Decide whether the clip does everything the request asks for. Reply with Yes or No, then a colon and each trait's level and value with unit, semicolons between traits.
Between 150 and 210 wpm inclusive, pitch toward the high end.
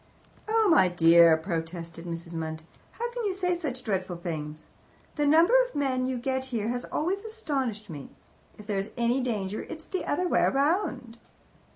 Yes: average, 175 wpm; high, 245 Hz